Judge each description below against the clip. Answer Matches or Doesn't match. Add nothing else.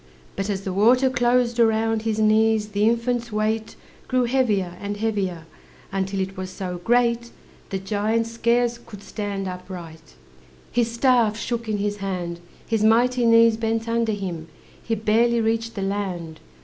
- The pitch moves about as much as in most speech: Matches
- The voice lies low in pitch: Doesn't match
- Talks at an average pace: Matches